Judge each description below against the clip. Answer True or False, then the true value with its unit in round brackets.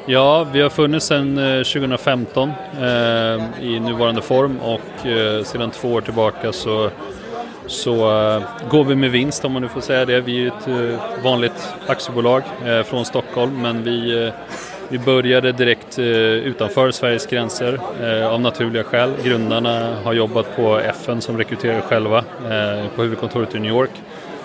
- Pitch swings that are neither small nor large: False (2.3 semitones)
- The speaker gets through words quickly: False (160 wpm)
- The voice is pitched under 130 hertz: True (120 Hz)